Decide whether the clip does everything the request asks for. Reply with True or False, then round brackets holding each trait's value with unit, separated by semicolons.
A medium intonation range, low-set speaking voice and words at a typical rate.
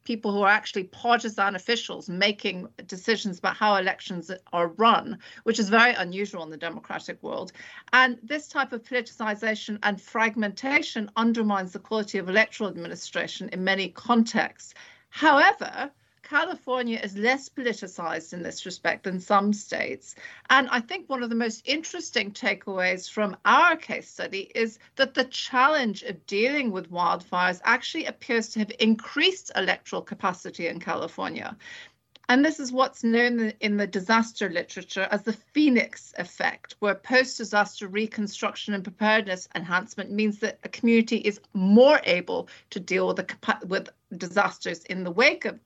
False (3.8 semitones; 215 Hz; 150 wpm)